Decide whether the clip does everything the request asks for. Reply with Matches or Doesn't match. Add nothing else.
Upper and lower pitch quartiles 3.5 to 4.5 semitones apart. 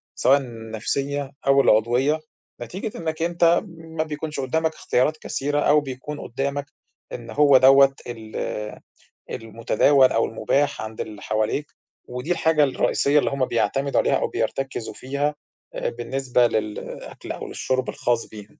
Matches